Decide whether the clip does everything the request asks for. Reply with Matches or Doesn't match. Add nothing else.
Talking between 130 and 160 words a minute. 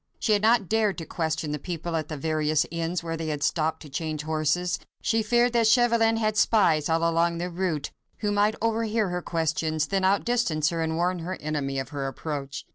Doesn't match